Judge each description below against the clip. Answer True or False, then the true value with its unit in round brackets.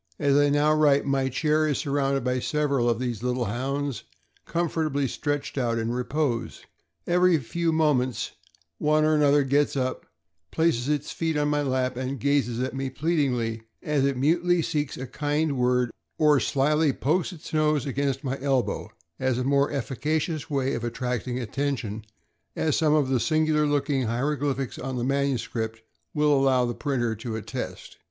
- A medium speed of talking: True (165 wpm)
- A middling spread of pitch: True (3.0 semitones)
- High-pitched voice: False (140 Hz)